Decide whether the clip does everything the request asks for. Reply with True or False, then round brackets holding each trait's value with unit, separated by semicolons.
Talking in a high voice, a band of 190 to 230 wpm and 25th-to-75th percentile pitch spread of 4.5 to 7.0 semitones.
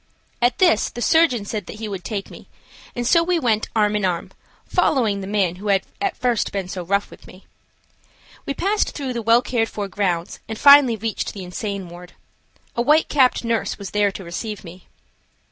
False (215 Hz; 200 wpm; 4.1 semitones)